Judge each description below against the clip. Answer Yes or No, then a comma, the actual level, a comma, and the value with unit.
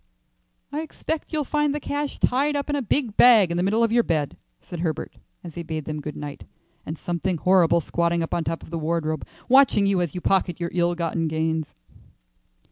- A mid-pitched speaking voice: Yes, medium, 175 Hz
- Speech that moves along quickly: Yes, fast, 210 wpm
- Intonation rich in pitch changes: Yes, wide, 6.8 semitones